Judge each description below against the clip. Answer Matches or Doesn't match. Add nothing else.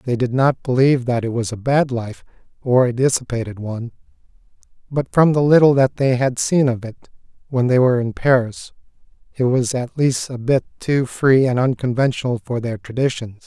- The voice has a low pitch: Matches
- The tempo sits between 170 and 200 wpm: Matches